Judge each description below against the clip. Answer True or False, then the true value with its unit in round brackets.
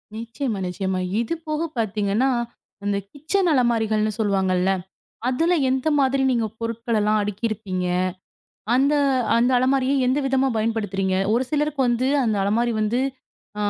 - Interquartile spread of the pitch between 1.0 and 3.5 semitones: False (4.1 semitones)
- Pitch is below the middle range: False (230 Hz)